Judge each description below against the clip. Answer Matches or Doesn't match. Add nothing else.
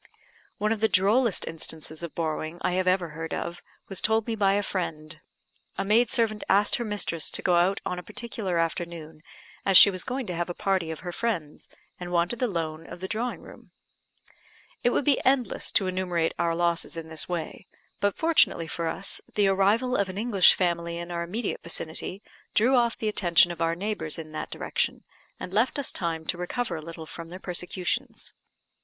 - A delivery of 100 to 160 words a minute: Doesn't match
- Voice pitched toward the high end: Doesn't match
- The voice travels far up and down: Doesn't match